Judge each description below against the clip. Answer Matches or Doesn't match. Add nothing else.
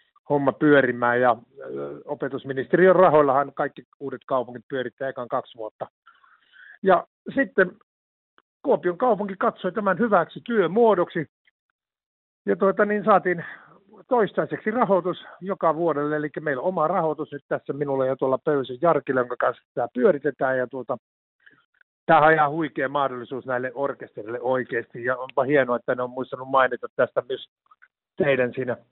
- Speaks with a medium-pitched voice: Matches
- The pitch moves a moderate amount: Doesn't match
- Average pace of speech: Matches